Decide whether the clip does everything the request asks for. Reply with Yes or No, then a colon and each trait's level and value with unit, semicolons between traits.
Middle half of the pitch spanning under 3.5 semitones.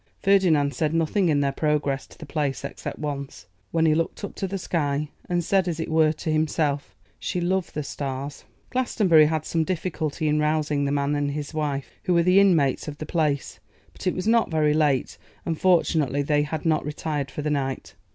Yes: average, 2.7 semitones